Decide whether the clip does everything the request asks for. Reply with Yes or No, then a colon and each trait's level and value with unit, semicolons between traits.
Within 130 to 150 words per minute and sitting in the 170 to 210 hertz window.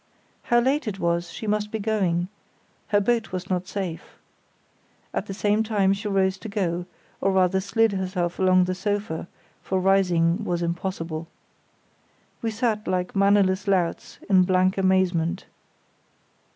Yes: average, 140 wpm; high, 190 Hz